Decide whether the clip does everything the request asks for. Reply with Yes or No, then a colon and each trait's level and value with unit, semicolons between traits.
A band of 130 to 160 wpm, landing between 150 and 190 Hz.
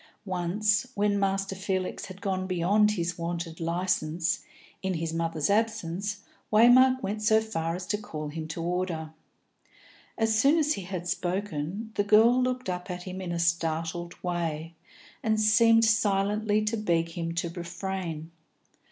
Yes: average, 150 wpm; medium, 185 Hz